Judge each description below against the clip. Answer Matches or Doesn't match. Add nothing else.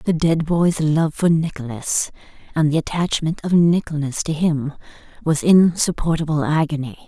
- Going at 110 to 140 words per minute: Matches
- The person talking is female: Matches